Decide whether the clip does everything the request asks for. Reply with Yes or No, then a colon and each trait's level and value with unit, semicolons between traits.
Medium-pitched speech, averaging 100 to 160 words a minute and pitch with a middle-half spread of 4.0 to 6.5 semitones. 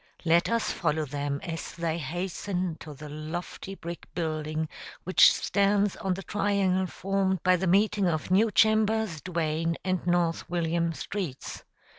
No: medium, 175 Hz; average, 145 wpm; average, 3.4 semitones